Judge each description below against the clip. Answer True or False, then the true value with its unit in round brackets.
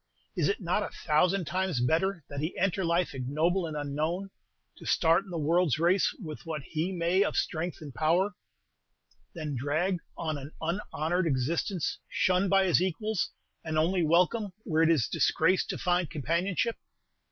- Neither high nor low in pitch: True (170 Hz)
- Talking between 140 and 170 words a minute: True (165 wpm)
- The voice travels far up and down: False (3.1 semitones)